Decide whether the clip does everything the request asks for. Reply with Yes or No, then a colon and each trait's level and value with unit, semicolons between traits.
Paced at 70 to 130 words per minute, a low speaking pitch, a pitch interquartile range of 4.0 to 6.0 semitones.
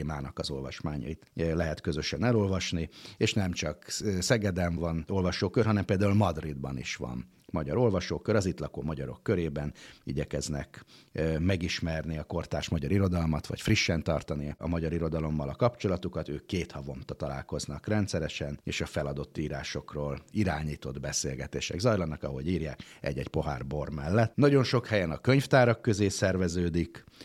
No: average, 140 wpm; very low, 85 Hz; average, 5.3 semitones